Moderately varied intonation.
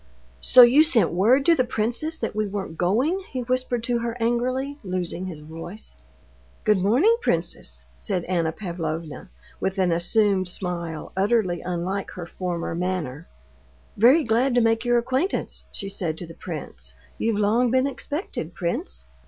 No: wide, 5.9 semitones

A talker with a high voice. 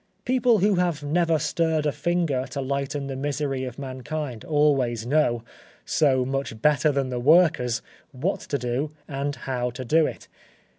No: medium, 140 Hz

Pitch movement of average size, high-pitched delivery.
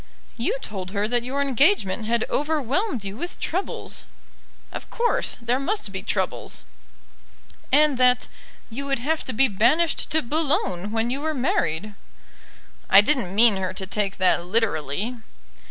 No: wide, 6.3 semitones; high, 240 Hz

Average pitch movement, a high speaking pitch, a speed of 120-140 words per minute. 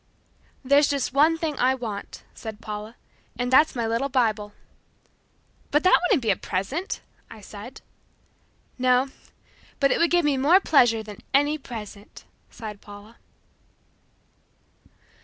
Yes: average, 5.0 semitones; very high, 250 Hz; slow, 135 wpm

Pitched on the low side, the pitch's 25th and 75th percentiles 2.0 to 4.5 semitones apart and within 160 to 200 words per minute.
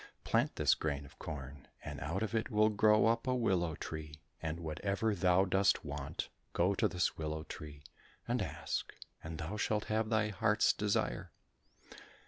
No: very low, 95 Hz; wide, 5.5 semitones; average, 165 wpm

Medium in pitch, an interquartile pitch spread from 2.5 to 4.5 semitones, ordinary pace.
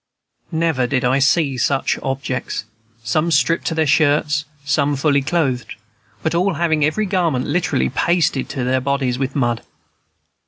Yes: medium, 145 Hz; average, 3.5 semitones; average, 150 wpm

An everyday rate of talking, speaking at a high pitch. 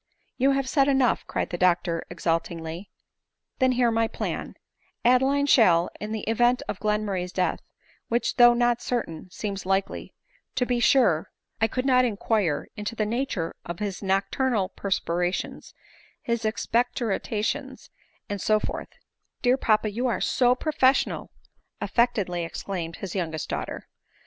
Yes: average, 150 wpm; high, 215 Hz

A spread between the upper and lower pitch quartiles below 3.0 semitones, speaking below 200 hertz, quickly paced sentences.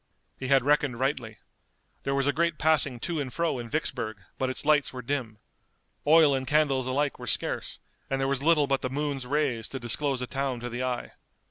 Yes: narrow, 2.6 semitones; low, 135 Hz; fast, 210 wpm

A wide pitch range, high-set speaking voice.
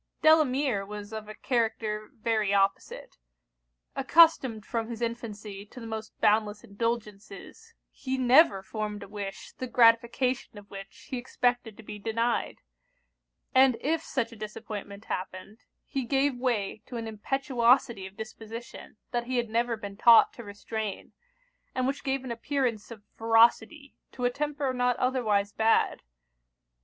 No: average, 3.2 semitones; high, 230 Hz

